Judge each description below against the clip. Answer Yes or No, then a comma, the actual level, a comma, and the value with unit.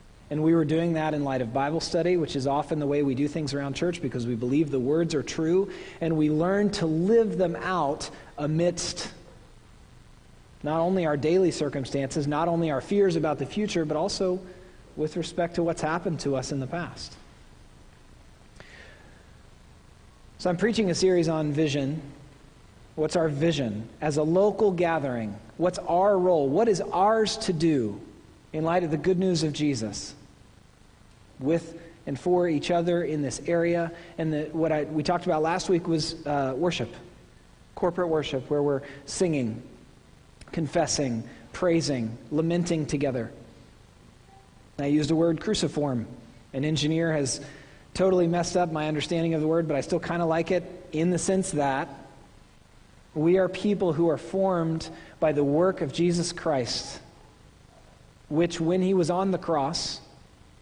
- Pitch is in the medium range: Yes, medium, 160 Hz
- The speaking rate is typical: Yes, average, 165 wpm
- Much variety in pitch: No, average, 3.5 semitones